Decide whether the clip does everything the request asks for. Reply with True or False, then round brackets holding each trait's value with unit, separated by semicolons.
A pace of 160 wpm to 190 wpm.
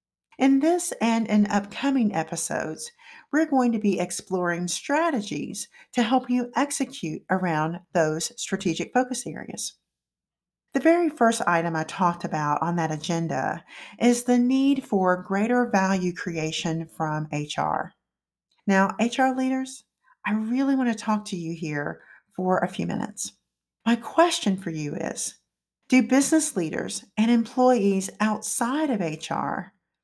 False (135 wpm)